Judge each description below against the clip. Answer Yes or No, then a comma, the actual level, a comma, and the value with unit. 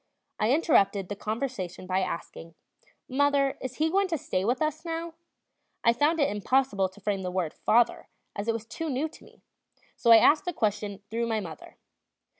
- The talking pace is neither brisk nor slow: Yes, average, 185 wpm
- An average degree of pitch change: No, wide, 6.3 semitones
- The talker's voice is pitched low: No, high, 230 Hz